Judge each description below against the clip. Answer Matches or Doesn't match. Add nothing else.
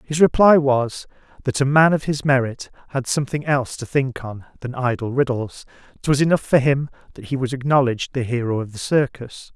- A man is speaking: Matches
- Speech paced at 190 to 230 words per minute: Matches